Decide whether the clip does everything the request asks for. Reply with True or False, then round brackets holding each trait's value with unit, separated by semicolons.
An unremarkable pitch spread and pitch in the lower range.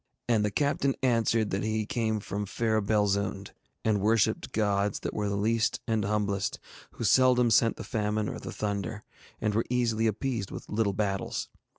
False (1.9 semitones; 110 Hz)